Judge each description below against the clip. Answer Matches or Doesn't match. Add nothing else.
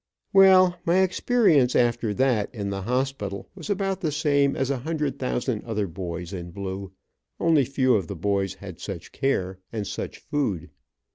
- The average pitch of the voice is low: Matches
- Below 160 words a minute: Doesn't match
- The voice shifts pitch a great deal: Matches